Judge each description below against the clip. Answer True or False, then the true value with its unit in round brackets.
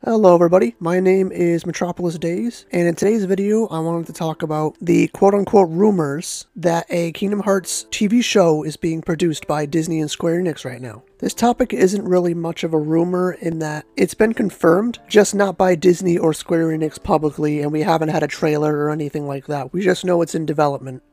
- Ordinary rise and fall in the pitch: True (3.4 semitones)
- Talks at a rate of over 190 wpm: True (205 wpm)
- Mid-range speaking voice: True (170 Hz)